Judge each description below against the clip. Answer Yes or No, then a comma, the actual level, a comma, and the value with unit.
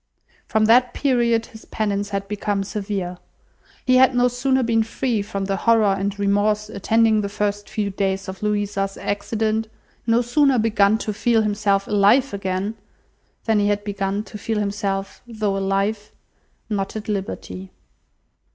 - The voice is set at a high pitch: Yes, high, 210 Hz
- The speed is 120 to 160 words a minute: Yes, average, 150 wpm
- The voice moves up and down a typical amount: No, narrow, 2.1 semitones